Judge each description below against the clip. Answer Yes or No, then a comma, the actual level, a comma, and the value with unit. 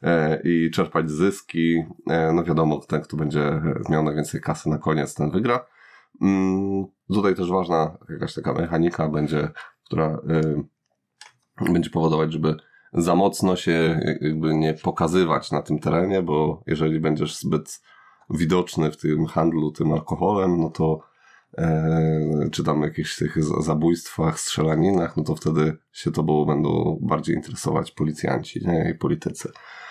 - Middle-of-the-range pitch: No, very low, 80 Hz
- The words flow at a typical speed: Yes, average, 130 wpm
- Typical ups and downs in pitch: No, narrow, 1.5 semitones